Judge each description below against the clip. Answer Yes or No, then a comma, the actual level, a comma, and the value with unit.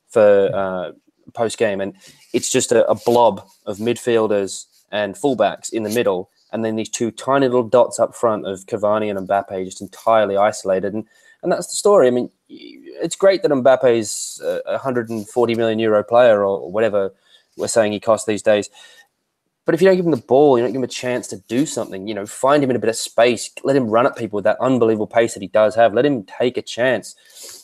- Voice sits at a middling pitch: No, low, 115 Hz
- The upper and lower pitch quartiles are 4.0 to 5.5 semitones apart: Yes, average, 4.5 semitones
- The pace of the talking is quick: Yes, fast, 220 wpm